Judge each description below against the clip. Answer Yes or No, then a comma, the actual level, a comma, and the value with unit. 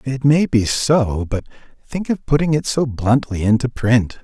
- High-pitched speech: No, low, 125 Hz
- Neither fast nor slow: Yes, average, 185 wpm